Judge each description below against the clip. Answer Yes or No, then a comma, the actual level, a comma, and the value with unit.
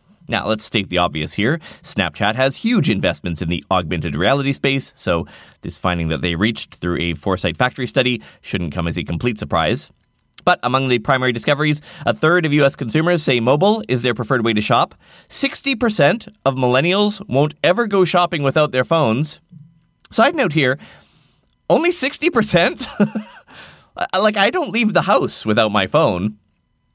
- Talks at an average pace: Yes, average, 165 wpm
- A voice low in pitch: Yes, low, 130 Hz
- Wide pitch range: Yes, wide, 8.7 semitones